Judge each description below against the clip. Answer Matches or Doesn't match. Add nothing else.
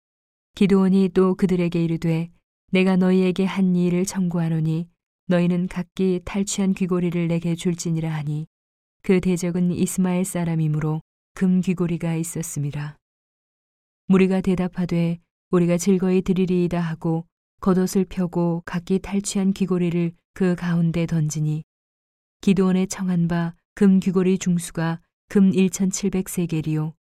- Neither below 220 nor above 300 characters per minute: Matches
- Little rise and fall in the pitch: Matches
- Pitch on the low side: Doesn't match